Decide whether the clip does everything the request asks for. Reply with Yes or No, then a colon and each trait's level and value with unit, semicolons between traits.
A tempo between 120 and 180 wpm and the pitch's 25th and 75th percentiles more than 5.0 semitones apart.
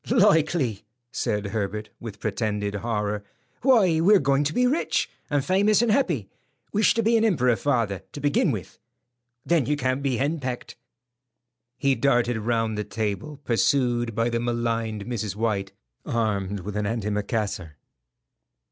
Yes: average, 145 wpm; wide, 5.6 semitones